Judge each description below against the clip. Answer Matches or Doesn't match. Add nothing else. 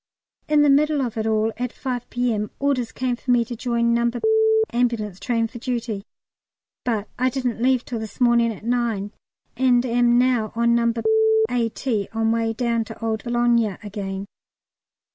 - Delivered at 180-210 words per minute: Doesn't match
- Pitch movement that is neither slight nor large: Doesn't match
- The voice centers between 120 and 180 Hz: Doesn't match